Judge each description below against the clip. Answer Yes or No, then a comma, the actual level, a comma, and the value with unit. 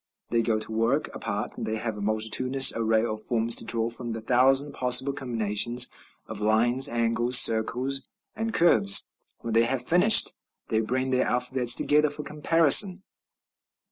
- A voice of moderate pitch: No, low, 120 Hz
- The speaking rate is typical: Yes, average, 155 wpm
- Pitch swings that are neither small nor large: Yes, average, 3.1 semitones